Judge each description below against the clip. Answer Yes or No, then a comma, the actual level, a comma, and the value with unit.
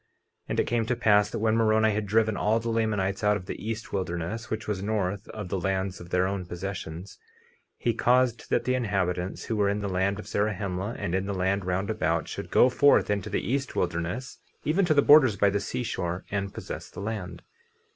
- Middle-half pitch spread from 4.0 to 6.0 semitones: No, average, 3.0 semitones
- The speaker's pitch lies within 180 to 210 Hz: No, low, 105 Hz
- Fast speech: Yes, fast, 215 wpm